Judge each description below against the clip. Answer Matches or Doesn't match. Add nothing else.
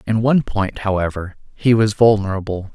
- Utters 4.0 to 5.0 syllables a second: Doesn't match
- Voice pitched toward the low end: Matches